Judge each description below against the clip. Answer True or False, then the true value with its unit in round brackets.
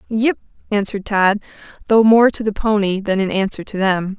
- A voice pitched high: True (205 Hz)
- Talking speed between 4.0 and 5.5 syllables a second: True (5.2 syllables/s)